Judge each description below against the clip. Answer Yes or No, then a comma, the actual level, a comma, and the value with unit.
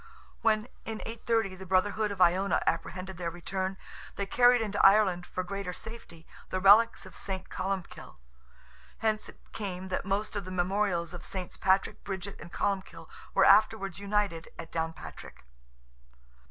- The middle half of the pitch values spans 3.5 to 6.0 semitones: No, narrow, 2.4 semitones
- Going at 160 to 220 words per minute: No, average, 150 wpm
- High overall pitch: Yes, high, 195 Hz